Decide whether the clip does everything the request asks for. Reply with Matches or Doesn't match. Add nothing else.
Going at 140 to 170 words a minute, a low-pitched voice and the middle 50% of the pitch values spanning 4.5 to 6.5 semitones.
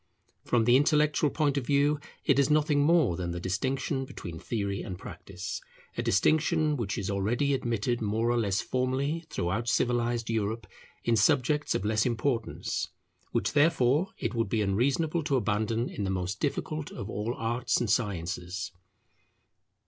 Matches